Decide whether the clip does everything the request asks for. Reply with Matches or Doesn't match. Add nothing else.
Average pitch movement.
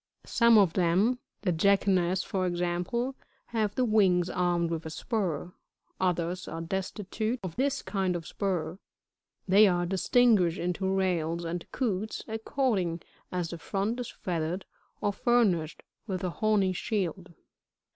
Matches